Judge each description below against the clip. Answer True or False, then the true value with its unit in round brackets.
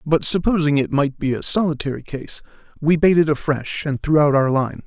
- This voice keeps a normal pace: True (195 wpm)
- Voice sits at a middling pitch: True (150 Hz)